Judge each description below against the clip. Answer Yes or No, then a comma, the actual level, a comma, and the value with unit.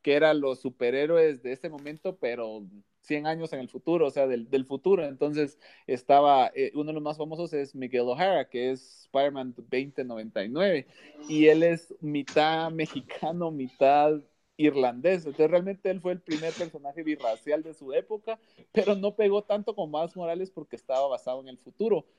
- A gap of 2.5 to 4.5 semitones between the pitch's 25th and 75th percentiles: Yes, average, 4.1 semitones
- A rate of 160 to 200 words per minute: Yes, average, 175 wpm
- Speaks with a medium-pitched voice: Yes, medium, 150 Hz